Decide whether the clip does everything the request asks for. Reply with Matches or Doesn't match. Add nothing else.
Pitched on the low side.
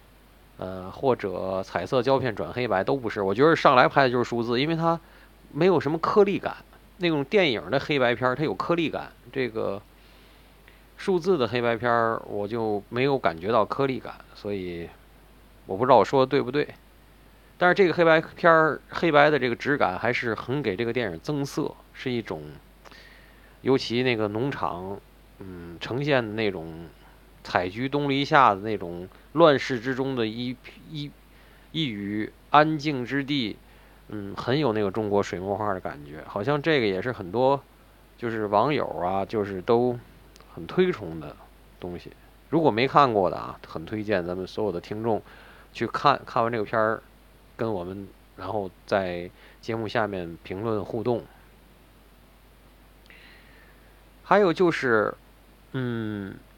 Matches